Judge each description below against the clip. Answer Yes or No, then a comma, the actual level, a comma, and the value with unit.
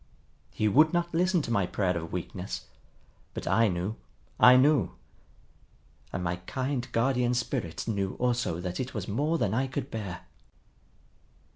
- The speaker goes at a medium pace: Yes, average, 150 wpm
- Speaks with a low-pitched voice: Yes, low, 115 Hz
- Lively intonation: Yes, wide, 5.9 semitones